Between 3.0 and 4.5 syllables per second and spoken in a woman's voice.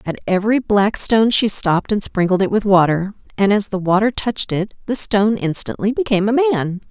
No: 5.7 syllables/s; female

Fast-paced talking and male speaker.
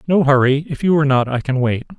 Yes: fast, 270 wpm; male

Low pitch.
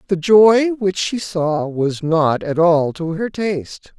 No: medium, 175 Hz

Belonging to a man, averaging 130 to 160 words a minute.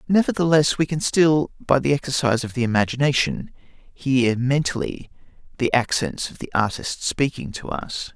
Yes: male; average, 145 wpm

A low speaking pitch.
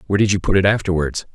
Yes: very low, 95 Hz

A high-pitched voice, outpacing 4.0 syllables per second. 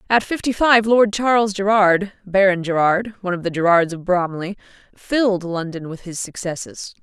Yes: high, 195 Hz; 5.0 syllables/s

